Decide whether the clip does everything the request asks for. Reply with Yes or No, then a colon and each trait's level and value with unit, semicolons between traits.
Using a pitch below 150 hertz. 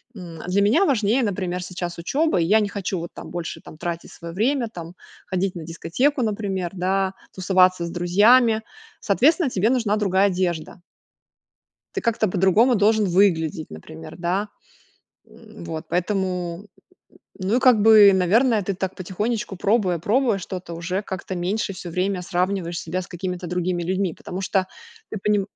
No: high, 190 Hz